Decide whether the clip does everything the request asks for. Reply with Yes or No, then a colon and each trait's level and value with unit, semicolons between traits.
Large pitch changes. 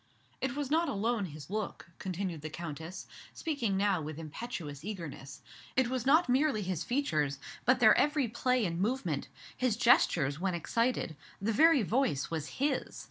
Yes: wide, 7.8 semitones